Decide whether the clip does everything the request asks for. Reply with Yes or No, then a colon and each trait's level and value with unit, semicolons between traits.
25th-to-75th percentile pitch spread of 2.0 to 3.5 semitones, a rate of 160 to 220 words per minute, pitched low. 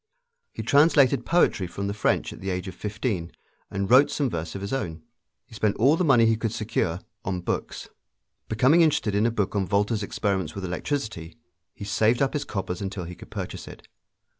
No: average, 4.7 semitones; average, 200 wpm; low, 105 Hz